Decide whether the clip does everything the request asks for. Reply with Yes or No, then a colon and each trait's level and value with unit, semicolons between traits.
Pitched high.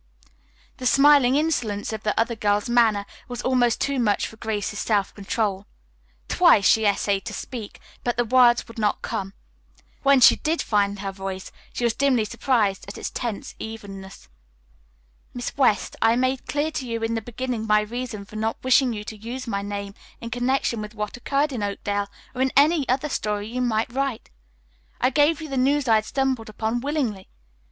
Yes: high, 230 Hz